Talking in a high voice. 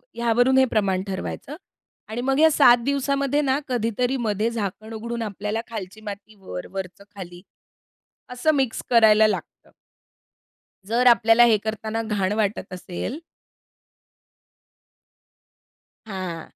Yes: high, 220 Hz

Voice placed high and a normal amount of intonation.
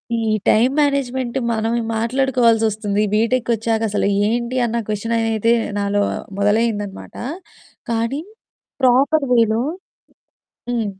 No: high, 230 Hz; narrow, 2.1 semitones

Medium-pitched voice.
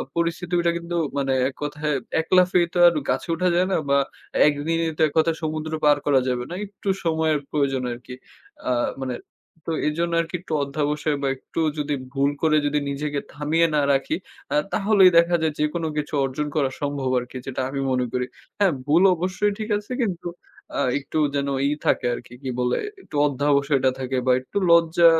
Yes: medium, 150 Hz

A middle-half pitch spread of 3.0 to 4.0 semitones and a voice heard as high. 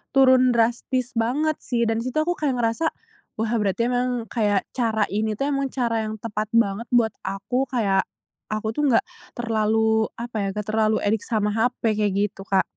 No: narrow, 2.5 semitones; high, 225 Hz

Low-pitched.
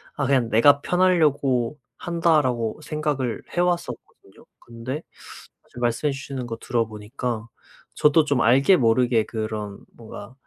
Yes: low, 125 Hz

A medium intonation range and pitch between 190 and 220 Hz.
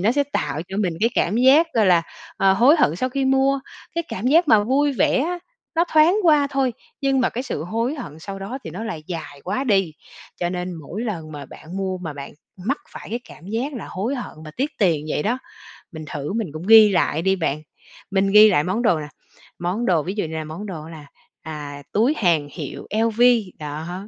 No: wide, 7.2 semitones; high, 200 Hz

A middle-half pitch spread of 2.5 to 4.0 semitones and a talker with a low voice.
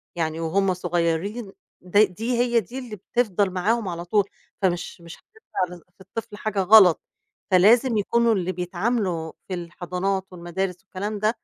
No: average, 3.6 semitones; high, 190 Hz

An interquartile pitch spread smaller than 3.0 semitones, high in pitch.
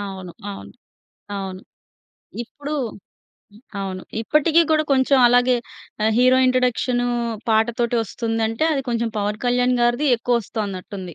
No: average, 3.5 semitones; high, 235 Hz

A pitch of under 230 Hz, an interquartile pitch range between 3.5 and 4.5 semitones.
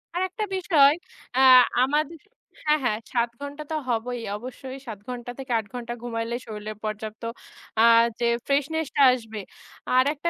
No: very high, 250 Hz; average, 4.0 semitones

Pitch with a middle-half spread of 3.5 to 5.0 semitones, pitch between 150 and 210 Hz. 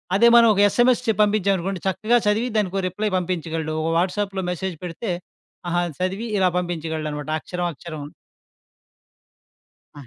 Yes: average, 3.8 semitones; medium, 185 Hz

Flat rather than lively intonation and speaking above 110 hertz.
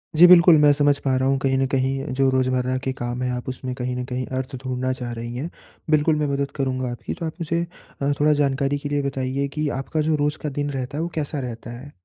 Yes: narrow, 2.2 semitones; low, 135 Hz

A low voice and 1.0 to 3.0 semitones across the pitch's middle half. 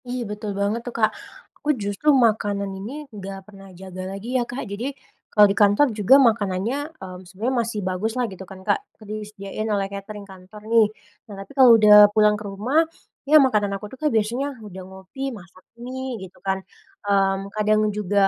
No: high, 205 Hz; narrow, 2.4 semitones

